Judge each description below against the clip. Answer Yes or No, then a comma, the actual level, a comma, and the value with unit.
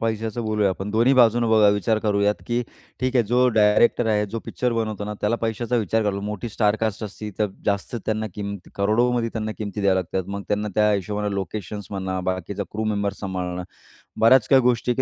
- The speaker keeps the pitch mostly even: Yes, narrow, 2.0 semitones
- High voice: No, low, 105 Hz